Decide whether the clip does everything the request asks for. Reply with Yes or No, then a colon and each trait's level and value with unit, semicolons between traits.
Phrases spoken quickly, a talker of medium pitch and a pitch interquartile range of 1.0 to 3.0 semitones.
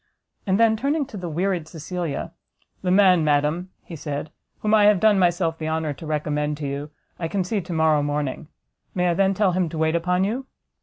No: fast, 210 wpm; medium, 175 Hz; average, 3.9 semitones